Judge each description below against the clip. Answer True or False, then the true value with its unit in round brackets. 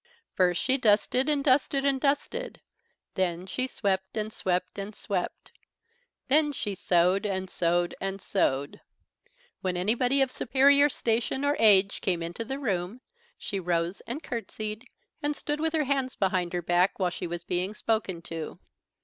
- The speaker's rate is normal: True (160 wpm)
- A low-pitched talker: False (205 Hz)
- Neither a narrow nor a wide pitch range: False (6.7 semitones)